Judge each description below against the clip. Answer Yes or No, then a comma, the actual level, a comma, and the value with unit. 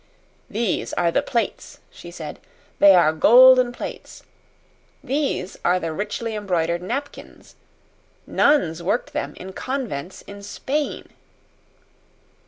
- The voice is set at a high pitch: Yes, high, 200 Hz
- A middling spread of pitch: No, wide, 6.6 semitones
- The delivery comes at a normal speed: No, slow, 110 wpm